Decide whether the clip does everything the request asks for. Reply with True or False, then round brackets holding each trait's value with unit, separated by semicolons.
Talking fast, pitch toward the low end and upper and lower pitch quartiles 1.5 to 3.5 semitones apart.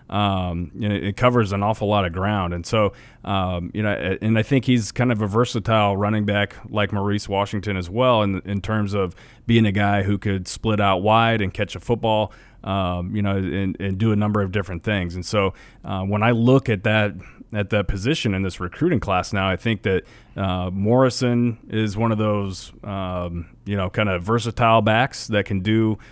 True (210 wpm; 105 Hz; 2.5 semitones)